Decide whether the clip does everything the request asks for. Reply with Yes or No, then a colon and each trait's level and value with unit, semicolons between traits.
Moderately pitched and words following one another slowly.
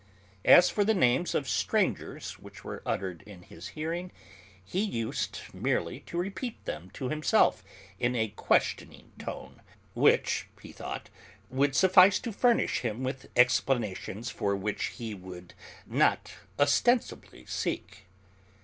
No: low, 130 Hz; slow, 130 wpm